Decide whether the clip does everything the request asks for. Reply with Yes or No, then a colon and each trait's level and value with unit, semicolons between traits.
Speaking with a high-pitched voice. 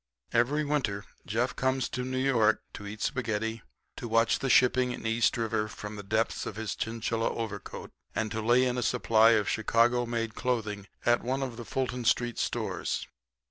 No: low, 115 Hz